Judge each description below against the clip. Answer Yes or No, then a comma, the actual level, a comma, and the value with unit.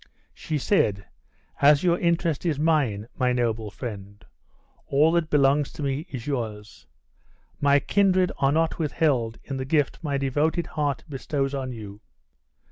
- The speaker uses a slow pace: No, average, 145 wpm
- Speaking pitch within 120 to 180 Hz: Yes, medium, 140 Hz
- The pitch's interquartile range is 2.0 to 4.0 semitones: No, average, 4.4 semitones